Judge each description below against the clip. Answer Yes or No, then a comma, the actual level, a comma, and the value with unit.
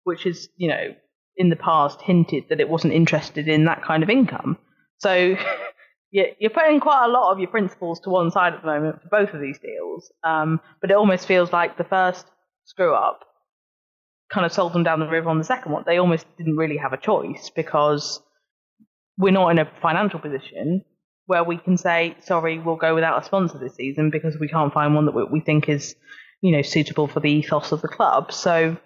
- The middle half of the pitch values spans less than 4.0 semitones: Yes, average, 3.0 semitones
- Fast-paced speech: Yes, fast, 215 wpm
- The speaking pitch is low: No, medium, 165 Hz